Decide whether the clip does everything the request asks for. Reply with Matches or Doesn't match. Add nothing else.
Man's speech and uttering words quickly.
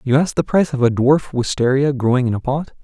Matches